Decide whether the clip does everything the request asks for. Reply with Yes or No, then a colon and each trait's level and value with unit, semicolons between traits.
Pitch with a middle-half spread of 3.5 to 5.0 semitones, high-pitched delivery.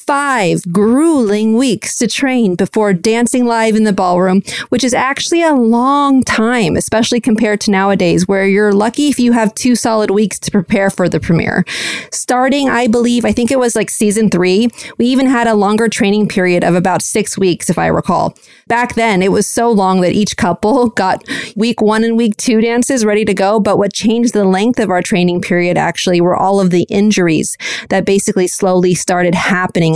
Yes: average, 3.8 semitones; high, 210 Hz